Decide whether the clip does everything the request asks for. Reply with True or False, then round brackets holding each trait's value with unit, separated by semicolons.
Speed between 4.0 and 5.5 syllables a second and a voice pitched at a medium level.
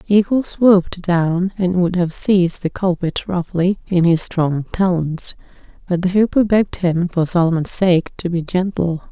True (4.6 syllables/s; 180 Hz)